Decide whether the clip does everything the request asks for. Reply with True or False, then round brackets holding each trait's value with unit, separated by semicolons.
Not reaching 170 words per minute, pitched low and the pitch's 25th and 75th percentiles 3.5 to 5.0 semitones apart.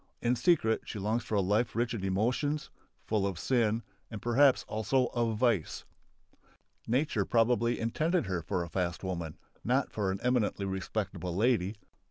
True (160 wpm; 110 Hz; 4.0 semitones)